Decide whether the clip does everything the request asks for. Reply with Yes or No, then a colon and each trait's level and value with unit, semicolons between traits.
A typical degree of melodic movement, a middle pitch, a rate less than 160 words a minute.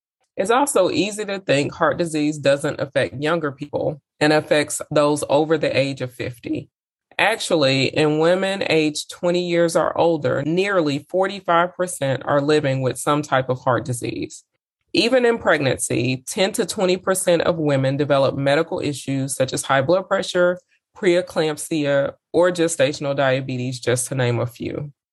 Yes: average, 4.4 semitones; medium, 150 Hz; average, 150 wpm